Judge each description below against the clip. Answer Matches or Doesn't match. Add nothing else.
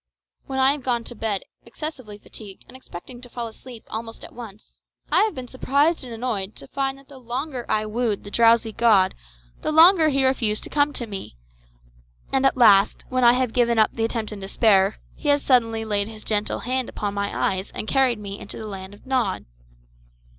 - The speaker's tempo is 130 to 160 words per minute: Doesn't match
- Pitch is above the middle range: Matches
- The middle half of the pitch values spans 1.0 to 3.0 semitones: Doesn't match